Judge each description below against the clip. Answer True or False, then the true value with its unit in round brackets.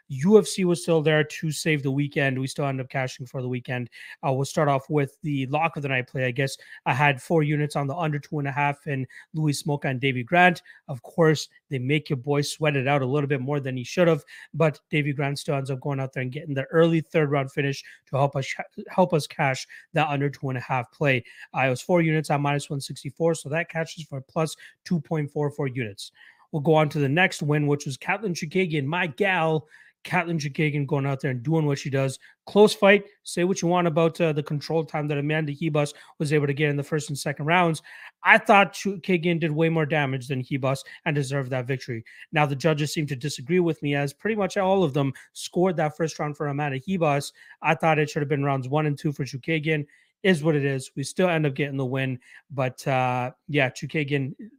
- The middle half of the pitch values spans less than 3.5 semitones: True (2.8 semitones)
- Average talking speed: False (235 wpm)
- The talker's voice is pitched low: False (150 Hz)